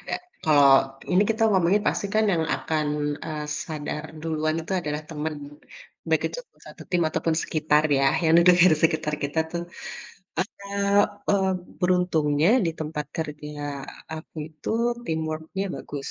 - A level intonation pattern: No, average, 3.0 semitones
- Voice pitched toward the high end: No, medium, 160 Hz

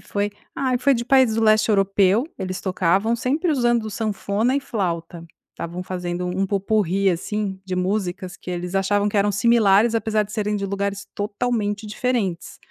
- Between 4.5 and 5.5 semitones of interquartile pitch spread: No, average, 2.9 semitones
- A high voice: Yes, high, 205 Hz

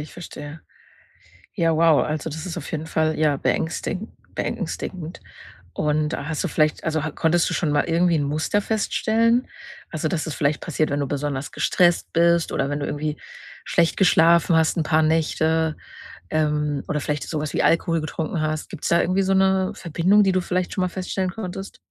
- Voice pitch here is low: No, medium, 160 Hz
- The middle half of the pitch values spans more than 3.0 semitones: No, average, 2.7 semitones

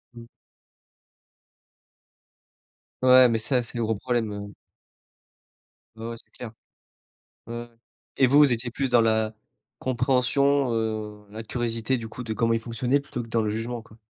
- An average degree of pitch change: No, narrow, 2.1 semitones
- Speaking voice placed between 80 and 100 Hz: No, low, 115 Hz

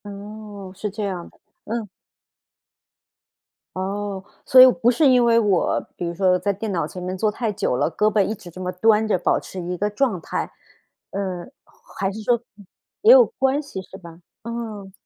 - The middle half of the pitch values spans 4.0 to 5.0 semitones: No, average, 3.3 semitones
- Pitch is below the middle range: No, high, 205 Hz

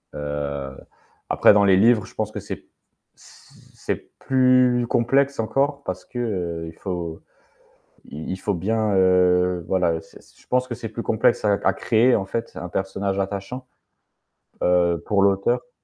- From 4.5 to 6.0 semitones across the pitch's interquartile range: Yes, average, 4.8 semitones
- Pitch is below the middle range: Yes, low, 100 Hz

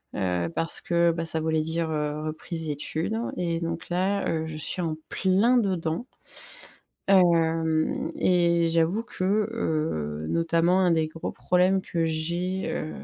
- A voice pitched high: No, medium, 165 Hz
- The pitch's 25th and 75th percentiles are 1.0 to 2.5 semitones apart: Yes, narrow, 2.2 semitones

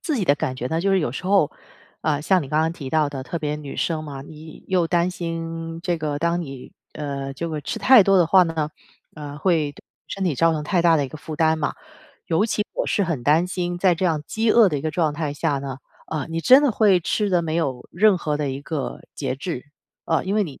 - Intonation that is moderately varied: Yes, average, 3.3 semitones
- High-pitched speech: No, medium, 160 Hz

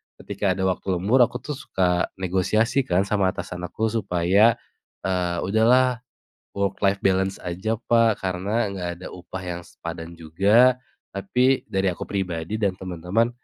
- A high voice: No, very low, 95 Hz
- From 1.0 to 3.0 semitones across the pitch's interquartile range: No, average, 3.6 semitones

